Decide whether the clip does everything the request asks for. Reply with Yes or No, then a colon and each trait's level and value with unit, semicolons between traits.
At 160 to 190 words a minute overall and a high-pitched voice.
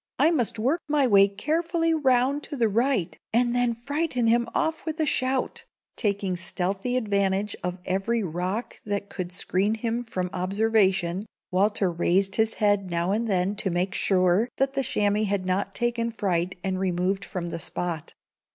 Yes: average, 170 wpm; high, 205 Hz